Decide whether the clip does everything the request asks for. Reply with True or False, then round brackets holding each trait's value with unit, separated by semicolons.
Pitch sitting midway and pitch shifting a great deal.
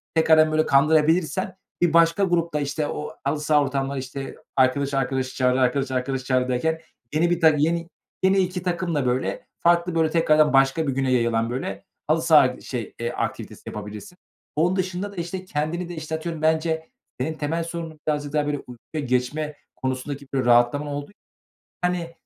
False (150 Hz; 3.8 semitones)